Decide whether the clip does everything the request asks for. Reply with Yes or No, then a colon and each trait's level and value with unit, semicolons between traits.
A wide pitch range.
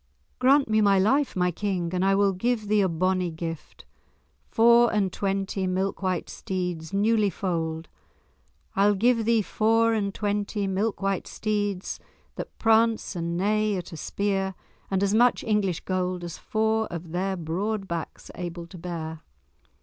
No: average, 3.1 semitones